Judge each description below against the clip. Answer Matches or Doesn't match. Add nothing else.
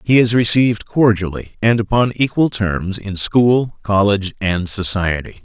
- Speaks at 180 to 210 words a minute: Doesn't match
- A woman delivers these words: Doesn't match